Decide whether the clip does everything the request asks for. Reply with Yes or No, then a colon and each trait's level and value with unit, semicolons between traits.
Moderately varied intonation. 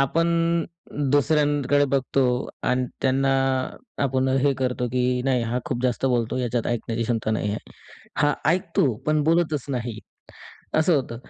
Yes: average, 3.3 semitones